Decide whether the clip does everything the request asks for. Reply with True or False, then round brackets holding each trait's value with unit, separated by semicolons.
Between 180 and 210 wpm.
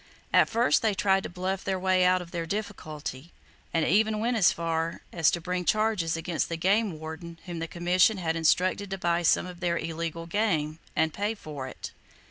True (200 wpm)